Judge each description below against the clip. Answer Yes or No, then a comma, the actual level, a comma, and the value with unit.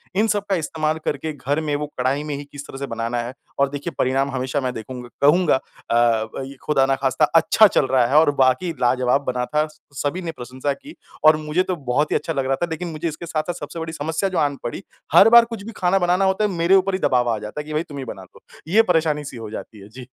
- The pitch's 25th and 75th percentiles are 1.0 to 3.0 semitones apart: No, average, 4.8 semitones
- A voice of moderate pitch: Yes, medium, 150 Hz